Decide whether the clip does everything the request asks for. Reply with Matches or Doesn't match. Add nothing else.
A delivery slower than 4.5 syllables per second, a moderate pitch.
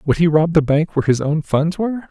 Doesn't match